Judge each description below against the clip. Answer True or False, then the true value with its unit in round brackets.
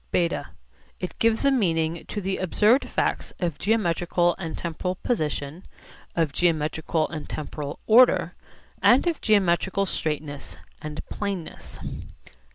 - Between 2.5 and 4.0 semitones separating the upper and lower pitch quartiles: False (4.5 semitones)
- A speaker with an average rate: False (120 wpm)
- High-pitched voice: False (175 Hz)